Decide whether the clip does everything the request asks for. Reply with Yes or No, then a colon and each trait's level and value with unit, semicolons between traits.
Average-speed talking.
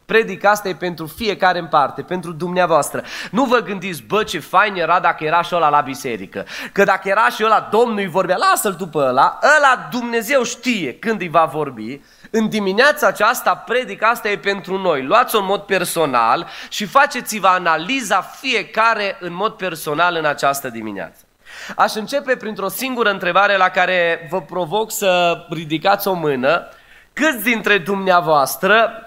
Yes: average, 160 wpm